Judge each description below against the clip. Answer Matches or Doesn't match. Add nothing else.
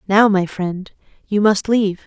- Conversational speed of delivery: Matches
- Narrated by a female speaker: Matches